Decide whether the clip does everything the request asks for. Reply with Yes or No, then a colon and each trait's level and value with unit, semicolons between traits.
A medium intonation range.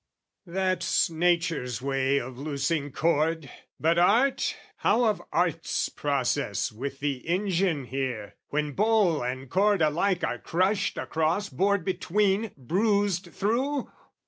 No: wide, 6.2 semitones